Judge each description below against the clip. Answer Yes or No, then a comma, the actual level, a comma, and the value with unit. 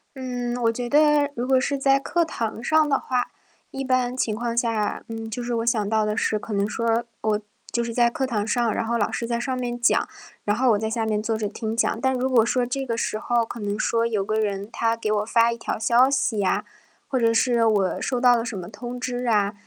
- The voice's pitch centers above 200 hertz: Yes, high, 235 Hz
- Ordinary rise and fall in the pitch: No, narrow, 2.2 semitones